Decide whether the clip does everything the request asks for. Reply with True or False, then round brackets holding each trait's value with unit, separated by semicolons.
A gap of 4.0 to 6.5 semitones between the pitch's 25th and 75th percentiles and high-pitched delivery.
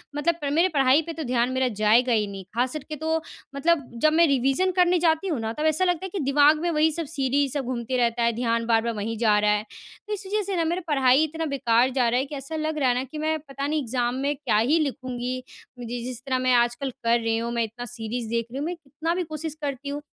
True (4.7 semitones; 270 Hz)